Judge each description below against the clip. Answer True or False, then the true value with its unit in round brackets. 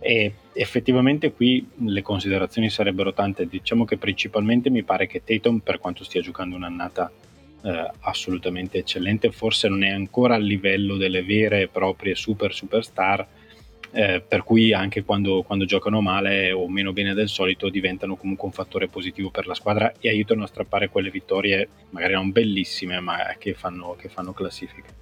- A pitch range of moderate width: False (2.3 semitones)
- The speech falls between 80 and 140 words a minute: False (170 wpm)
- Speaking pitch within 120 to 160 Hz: False (100 Hz)